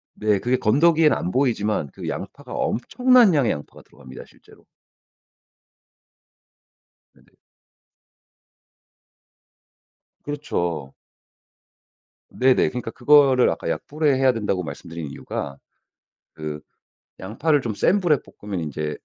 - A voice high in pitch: No, low, 120 Hz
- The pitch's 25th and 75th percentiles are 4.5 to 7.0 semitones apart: No, wide, 9.0 semitones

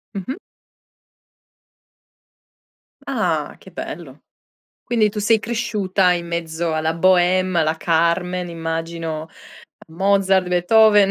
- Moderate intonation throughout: Yes, average, 3.2 semitones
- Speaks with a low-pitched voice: No, medium, 180 Hz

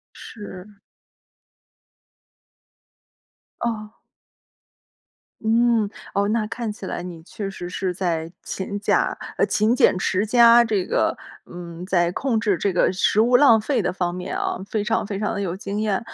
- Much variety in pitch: No, average, 3.5 semitones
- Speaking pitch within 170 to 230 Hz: Yes, high, 205 Hz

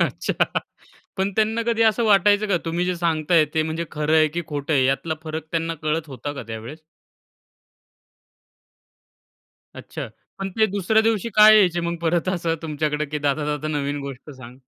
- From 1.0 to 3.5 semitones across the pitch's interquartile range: No, average, 4.3 semitones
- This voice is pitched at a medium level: Yes, medium, 165 Hz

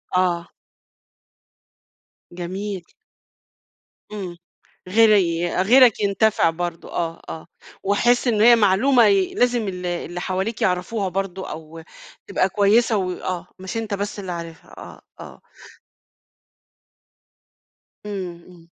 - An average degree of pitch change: Yes, average, 3.2 semitones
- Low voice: No, high, 190 Hz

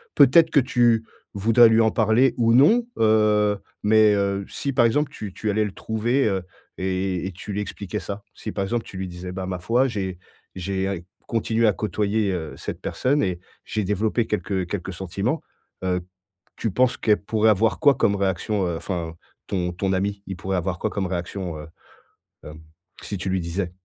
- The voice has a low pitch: Yes, low, 100 Hz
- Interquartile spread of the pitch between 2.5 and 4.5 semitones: Yes, average, 3.1 semitones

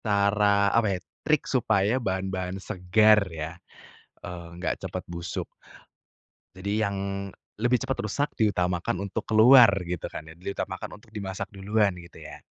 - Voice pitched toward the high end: No, low, 100 Hz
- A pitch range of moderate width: Yes, average, 3.0 semitones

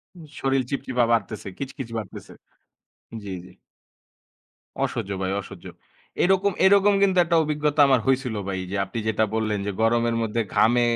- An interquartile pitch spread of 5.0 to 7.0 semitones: Yes, wide, 5.4 semitones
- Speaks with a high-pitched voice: No, low, 120 Hz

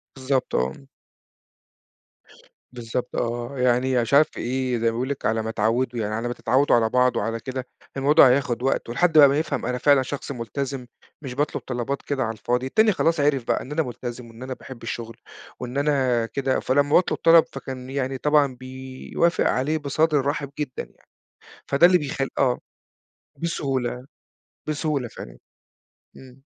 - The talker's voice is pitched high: No, low, 130 Hz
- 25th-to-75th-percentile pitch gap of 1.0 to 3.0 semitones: Yes, average, 2.7 semitones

